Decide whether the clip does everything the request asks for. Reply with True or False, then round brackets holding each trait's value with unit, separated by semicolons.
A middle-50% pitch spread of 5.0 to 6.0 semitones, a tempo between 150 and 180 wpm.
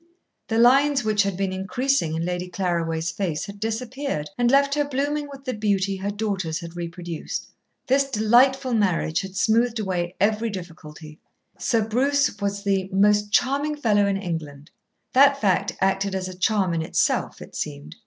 True (5.4 semitones; 165 wpm)